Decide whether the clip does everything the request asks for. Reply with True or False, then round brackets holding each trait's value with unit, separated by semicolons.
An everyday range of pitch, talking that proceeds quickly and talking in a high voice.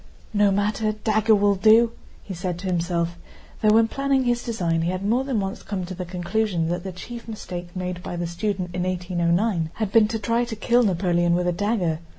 True (3.8 semitones; 215 wpm; 195 Hz)